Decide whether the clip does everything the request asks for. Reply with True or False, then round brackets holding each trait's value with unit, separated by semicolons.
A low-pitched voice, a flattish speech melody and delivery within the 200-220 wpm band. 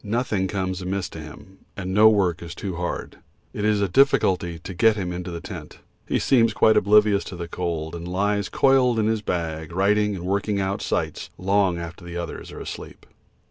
False (95 Hz; 3.1 semitones; 205 wpm)